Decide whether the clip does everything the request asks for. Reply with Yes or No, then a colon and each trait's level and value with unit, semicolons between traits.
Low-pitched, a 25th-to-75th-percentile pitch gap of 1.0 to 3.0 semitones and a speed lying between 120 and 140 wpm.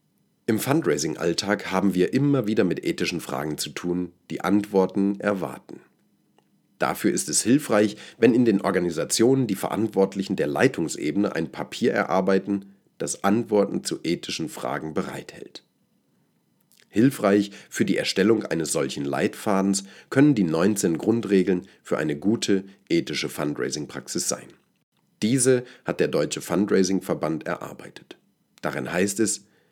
Yes: very low, 95 Hz; narrow, 2.4 semitones; slow, 125 wpm